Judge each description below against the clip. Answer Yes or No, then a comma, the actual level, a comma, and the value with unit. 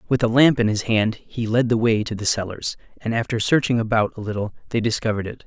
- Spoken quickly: Yes, fast, 240 wpm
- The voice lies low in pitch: Yes, low, 115 Hz